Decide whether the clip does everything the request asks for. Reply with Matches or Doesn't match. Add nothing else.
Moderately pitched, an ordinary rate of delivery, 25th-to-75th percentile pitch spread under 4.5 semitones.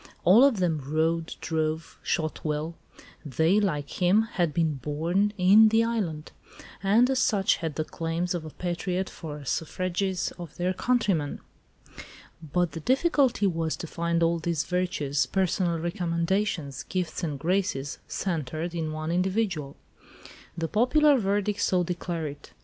Matches